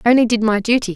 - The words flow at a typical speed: No, fast, 250 wpm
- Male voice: No, female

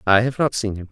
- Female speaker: No, male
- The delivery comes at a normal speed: No, fast, 330 wpm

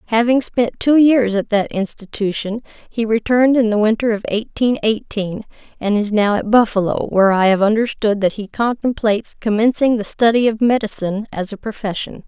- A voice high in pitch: Yes, high, 220 Hz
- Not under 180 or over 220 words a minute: No, average, 170 wpm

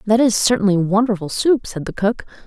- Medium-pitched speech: No, high, 210 Hz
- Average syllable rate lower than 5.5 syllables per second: No, 5.6 syllables/s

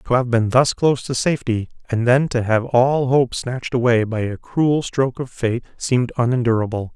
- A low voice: Yes, low, 125 Hz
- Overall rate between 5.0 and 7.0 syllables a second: Yes, 5.3 syllables/s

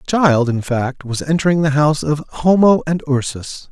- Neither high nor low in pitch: Yes, medium, 145 Hz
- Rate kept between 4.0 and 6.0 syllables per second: Yes, 4.8 syllables/s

